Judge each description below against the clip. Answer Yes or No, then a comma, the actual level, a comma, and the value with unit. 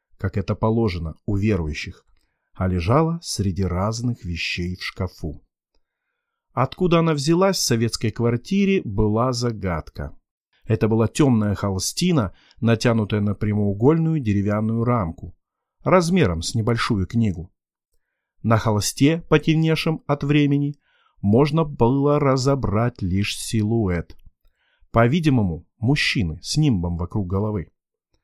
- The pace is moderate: No, slow, 105 wpm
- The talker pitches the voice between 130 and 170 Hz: No, low, 115 Hz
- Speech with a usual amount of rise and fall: No, wide, 6.7 semitones